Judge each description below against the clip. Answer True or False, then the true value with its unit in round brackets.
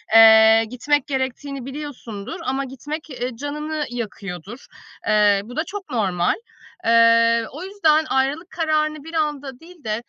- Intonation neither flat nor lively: True (4.9 semitones)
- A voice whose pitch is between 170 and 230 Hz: False (265 Hz)